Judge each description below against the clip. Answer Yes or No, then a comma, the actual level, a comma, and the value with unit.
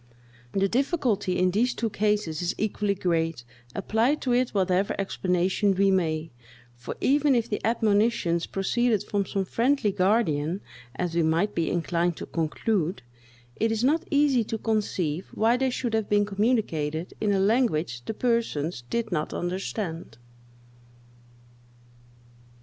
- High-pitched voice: Yes, high, 200 Hz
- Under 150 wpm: Yes, average, 140 wpm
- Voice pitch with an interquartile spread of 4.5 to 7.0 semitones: Yes, average, 4.8 semitones